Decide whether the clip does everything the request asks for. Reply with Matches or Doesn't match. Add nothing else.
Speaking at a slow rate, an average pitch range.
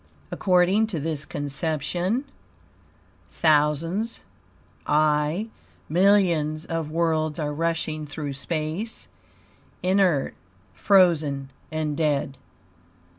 Matches